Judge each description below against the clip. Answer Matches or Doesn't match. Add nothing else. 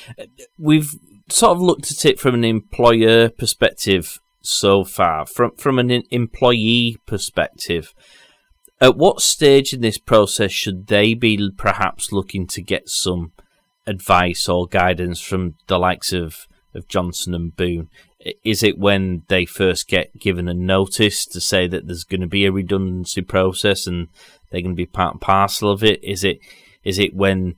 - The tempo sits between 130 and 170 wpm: Matches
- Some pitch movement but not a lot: Matches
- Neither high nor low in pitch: Doesn't match